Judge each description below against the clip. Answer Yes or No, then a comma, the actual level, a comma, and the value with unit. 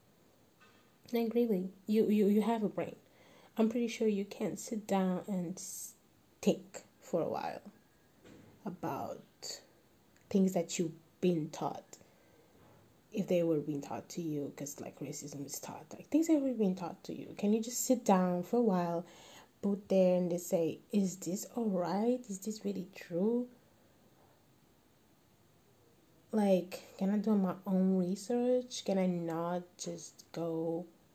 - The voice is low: No, medium, 185 Hz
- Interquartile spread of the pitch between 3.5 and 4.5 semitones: Yes, average, 4.1 semitones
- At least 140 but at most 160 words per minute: Yes, average, 150 wpm